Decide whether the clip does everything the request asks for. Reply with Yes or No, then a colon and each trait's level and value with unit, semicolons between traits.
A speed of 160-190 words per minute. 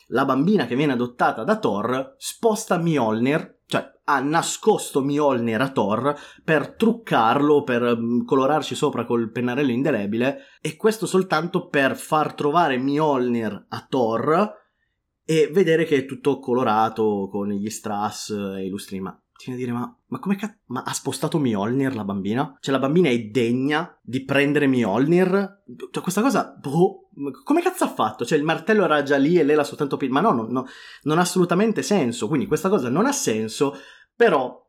Yes: fast, 170 wpm